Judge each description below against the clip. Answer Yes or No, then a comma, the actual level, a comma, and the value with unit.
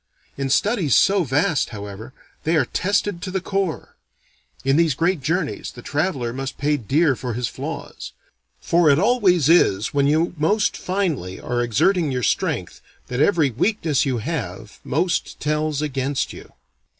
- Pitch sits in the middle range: Yes, medium, 150 Hz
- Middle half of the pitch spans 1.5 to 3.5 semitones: No, wide, 5.4 semitones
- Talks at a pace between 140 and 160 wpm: Yes, average, 155 wpm